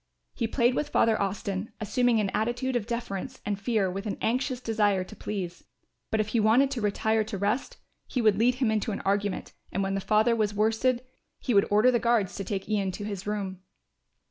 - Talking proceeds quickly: Yes, fast, 210 wpm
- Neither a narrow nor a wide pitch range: Yes, average, 3.1 semitones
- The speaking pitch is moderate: No, high, 215 Hz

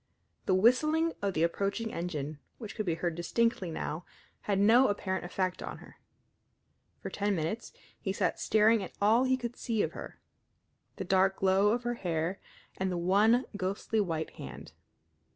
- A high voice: Yes, high, 200 Hz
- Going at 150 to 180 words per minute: Yes, average, 170 wpm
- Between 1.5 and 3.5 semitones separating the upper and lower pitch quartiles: No, average, 4.2 semitones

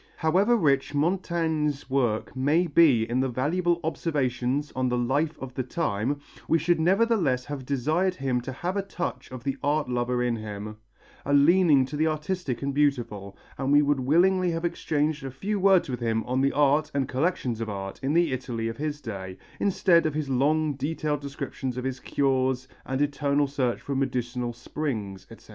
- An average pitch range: Yes, average, 4.0 semitones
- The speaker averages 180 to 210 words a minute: Yes, average, 185 wpm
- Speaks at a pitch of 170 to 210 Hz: No, medium, 140 Hz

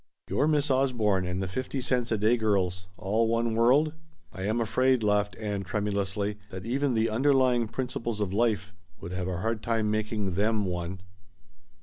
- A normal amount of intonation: Yes, average, 3.4 semitones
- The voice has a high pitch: No, low, 110 Hz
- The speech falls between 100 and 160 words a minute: No, average, 175 wpm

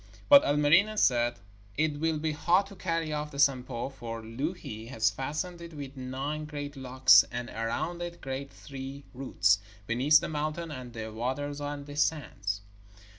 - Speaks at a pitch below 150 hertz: Yes, medium, 140 Hz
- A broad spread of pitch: No, average, 3.7 semitones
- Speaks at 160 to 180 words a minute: Yes, average, 165 wpm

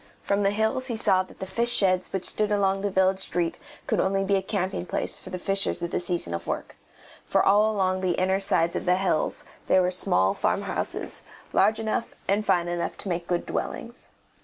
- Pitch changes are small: Yes, narrow, 2.1 semitones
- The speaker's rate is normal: No, fast, 215 wpm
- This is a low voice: No, high, 190 Hz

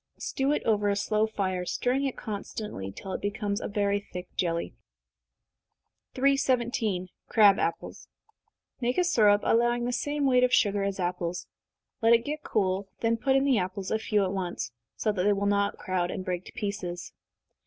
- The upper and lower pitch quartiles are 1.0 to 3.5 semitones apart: No, average, 4.2 semitones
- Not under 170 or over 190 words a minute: Yes, average, 175 wpm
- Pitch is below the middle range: No, high, 205 Hz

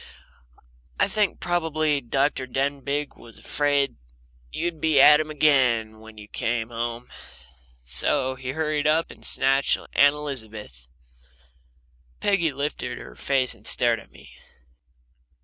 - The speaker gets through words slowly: Yes, slow, 125 wpm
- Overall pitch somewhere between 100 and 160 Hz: Yes, low, 135 Hz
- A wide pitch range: No, average, 4.2 semitones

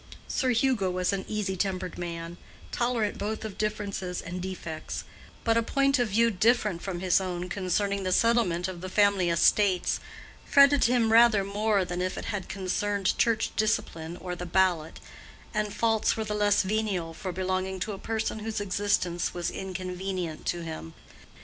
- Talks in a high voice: Yes, high, 195 Hz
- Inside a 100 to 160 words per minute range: No, average, 170 wpm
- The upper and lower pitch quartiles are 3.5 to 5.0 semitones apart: No, average, 3.1 semitones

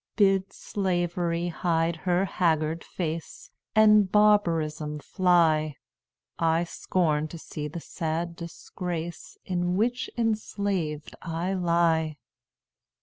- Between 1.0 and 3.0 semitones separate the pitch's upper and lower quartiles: Yes, narrow, 2.5 semitones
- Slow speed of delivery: Yes, slow, 95 wpm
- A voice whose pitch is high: No, medium, 170 Hz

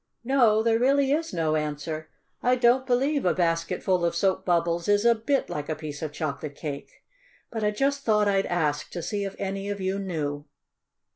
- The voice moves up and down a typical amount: No, wide, 6.6 semitones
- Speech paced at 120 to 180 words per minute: No, average, 200 wpm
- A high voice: Yes, high, 195 Hz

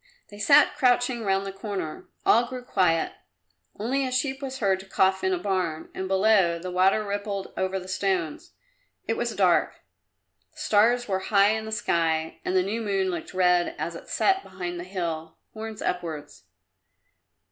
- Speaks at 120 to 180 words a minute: Yes, average, 175 wpm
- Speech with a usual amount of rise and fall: Yes, average, 3.5 semitones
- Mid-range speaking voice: No, high, 195 Hz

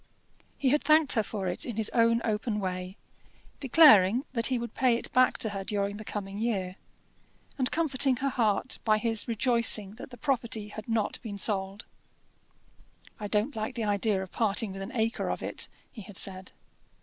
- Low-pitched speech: No, high, 220 Hz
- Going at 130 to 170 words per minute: No, average, 185 wpm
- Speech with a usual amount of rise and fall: Yes, average, 3.4 semitones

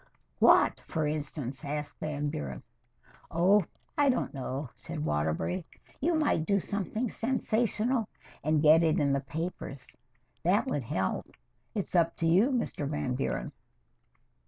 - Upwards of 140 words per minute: No, slow, 135 wpm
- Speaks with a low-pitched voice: No, medium, 155 Hz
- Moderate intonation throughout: No, wide, 6.7 semitones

